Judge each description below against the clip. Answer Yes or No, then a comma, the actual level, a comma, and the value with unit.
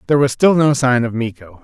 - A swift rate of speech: Yes, fast, 255 wpm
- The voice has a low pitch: Yes, low, 130 Hz